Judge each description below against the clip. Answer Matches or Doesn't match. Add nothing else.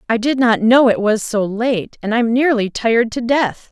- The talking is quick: Matches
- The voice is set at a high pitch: Matches